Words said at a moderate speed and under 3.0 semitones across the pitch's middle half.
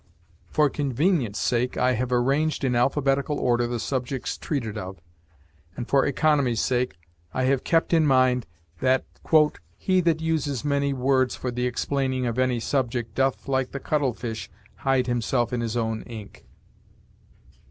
Yes: average, 150 wpm; narrow, 2.5 semitones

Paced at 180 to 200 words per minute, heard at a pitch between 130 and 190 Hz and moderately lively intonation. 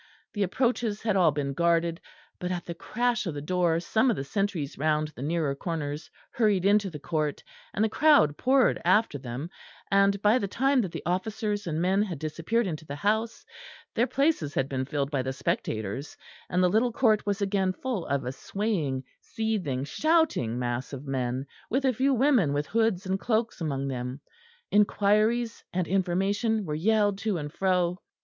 No: average, 185 wpm; medium, 185 Hz; wide, 6.7 semitones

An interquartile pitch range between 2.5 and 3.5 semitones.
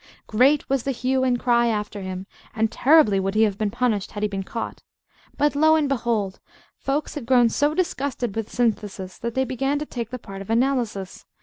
No: average, 4.5 semitones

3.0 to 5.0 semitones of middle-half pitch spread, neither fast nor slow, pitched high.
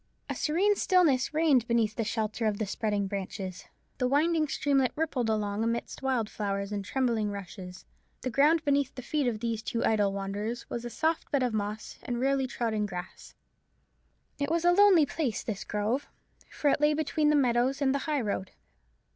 No: wide, 5.4 semitones; average, 185 wpm; high, 240 Hz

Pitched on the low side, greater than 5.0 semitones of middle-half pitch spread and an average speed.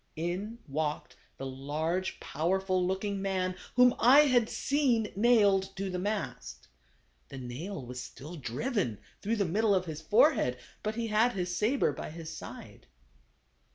No: high, 190 Hz; wide, 5.5 semitones; average, 155 wpm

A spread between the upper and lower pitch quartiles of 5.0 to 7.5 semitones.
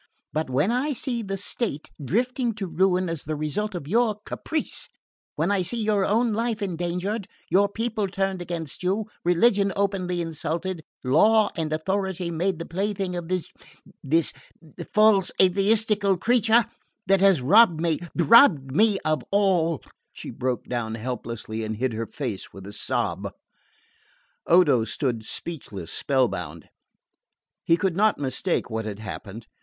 Yes: average, 5.3 semitones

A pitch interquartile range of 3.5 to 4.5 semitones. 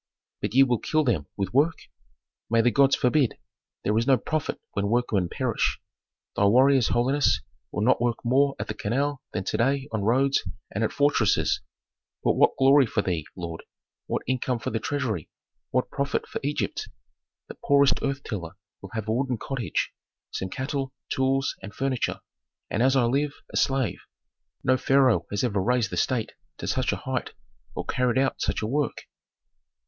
Yes: average, 4.0 semitones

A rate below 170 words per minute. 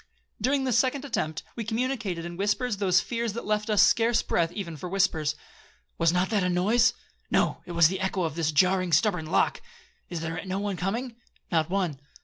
No: average, 185 wpm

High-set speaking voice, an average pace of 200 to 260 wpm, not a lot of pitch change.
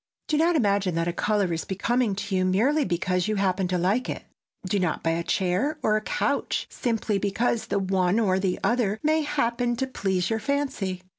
No: high, 200 Hz; fast, 205 wpm; average, 4.5 semitones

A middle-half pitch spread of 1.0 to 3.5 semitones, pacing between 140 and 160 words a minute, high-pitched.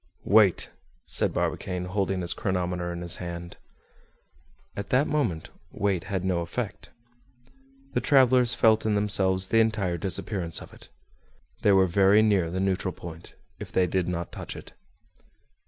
No: average, 3.0 semitones; average, 150 wpm; very low, 95 Hz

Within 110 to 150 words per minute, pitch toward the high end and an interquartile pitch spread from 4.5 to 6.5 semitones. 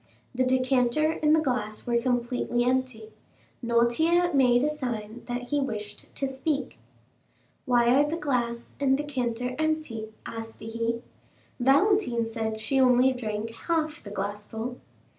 No: slow, 135 wpm; high, 245 Hz; average, 3.3 semitones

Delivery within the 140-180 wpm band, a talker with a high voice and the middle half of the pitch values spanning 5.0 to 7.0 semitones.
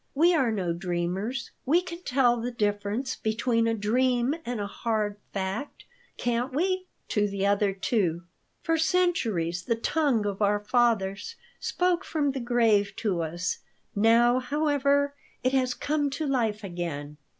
Yes: average, 150 wpm; high, 230 Hz; average, 5.3 semitones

